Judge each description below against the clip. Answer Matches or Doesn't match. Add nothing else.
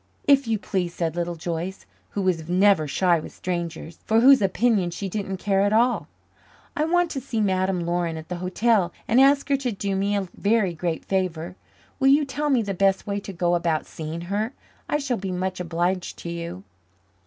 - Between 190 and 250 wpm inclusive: Matches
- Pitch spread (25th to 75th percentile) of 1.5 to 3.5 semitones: Doesn't match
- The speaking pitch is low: Doesn't match